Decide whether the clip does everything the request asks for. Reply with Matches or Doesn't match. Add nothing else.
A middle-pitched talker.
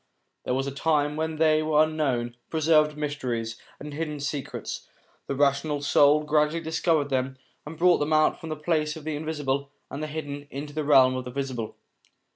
Matches